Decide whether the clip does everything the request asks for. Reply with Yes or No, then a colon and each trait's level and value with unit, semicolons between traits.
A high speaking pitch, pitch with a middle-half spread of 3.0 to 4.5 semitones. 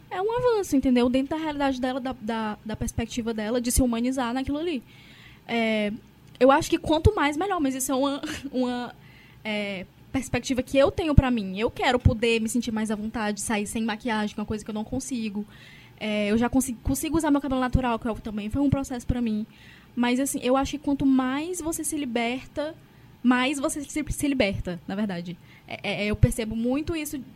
Yes: very high, 250 Hz; average, 4.2 semitones